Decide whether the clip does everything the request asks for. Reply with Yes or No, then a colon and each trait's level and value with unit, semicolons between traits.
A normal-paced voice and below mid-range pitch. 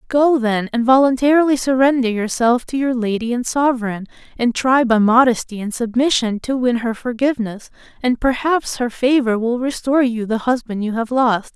No: average, 170 wpm; high, 245 Hz